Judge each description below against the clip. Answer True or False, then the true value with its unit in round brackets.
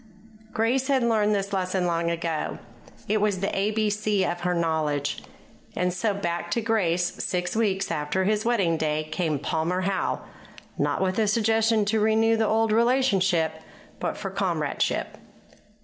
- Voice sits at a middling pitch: False (195 Hz)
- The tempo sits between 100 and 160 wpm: True (150 wpm)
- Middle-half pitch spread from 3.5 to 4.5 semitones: True (4.1 semitones)